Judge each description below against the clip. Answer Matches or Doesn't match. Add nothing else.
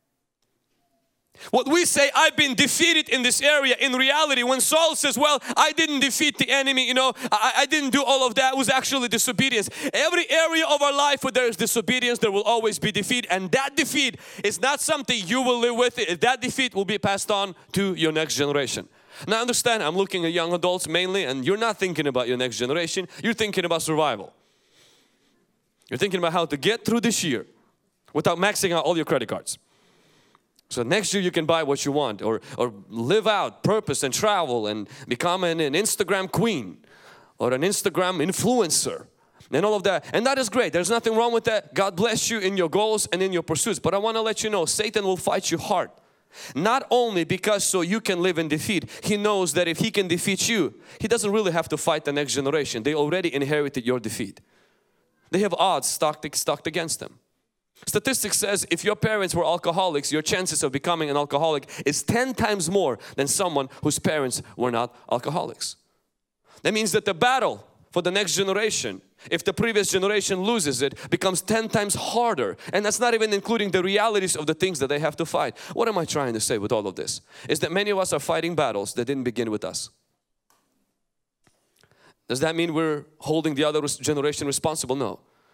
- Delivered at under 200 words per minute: Doesn't match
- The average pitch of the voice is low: Doesn't match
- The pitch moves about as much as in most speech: Doesn't match